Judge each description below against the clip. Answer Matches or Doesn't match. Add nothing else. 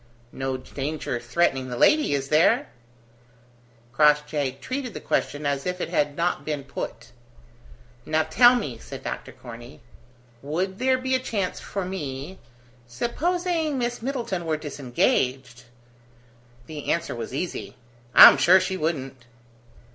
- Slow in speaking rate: Matches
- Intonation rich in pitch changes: Matches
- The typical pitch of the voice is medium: Matches